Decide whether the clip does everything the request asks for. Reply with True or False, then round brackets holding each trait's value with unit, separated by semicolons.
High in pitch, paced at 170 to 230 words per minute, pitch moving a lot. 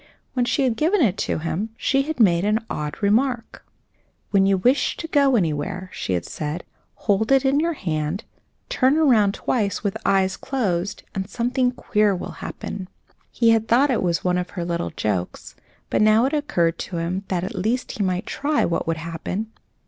True (205 Hz; 190 wpm; 6.2 semitones)